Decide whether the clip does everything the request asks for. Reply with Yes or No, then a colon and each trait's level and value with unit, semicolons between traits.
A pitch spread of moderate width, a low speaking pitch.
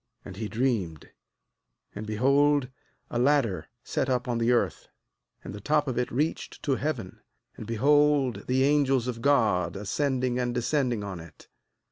Yes: average, 4.4 semitones; low, 125 Hz